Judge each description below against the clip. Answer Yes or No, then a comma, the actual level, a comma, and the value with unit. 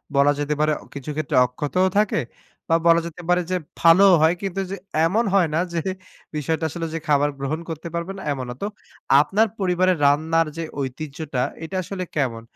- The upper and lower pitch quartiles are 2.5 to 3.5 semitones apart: No, average, 3.9 semitones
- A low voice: No, medium, 165 Hz